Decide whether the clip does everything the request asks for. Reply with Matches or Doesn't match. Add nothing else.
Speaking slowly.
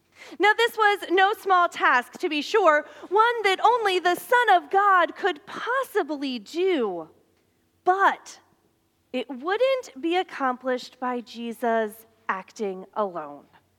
Matches